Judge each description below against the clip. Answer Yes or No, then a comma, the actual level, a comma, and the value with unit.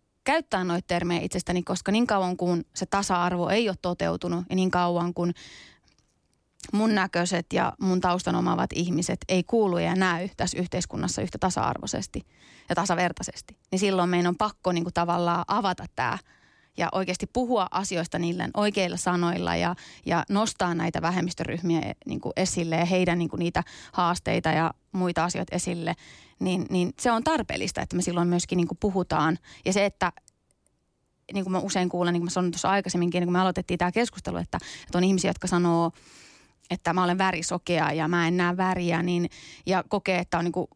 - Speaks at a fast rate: Yes, fast, 175 wpm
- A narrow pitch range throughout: Yes, narrow, 1.5 semitones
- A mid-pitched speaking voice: Yes, medium, 180 Hz